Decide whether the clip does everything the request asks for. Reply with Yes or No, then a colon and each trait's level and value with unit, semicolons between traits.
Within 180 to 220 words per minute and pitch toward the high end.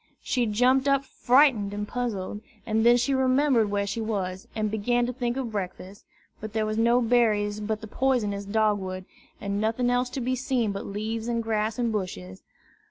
Yes: average, 190 wpm; high, 220 Hz